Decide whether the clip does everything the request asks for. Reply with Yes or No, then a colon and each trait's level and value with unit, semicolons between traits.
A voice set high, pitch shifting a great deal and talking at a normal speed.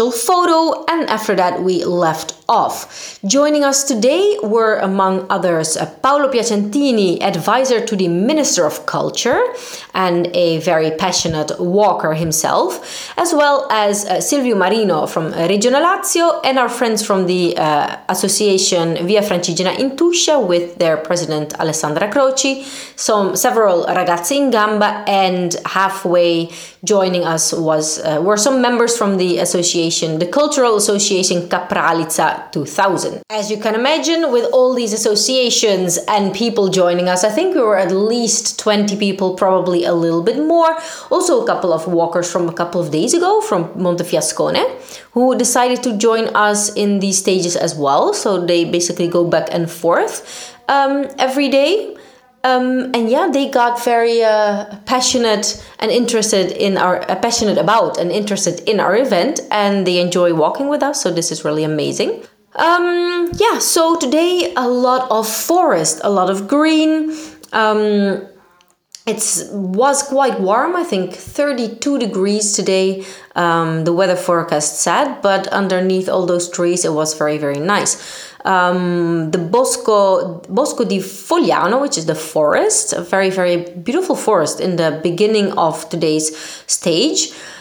Yes: high, 205 Hz; wide, 6.5 semitones; average, 150 wpm